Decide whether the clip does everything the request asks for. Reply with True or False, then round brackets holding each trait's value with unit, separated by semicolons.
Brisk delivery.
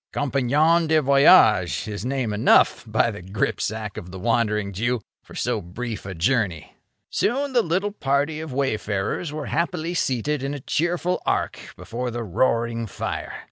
False (155 wpm)